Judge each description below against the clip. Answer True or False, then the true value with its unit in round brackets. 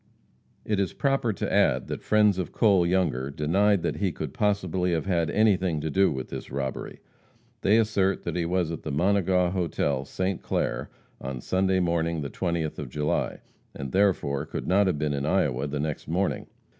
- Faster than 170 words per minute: True (185 wpm)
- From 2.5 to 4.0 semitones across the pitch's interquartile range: False (4.5 semitones)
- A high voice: False (90 Hz)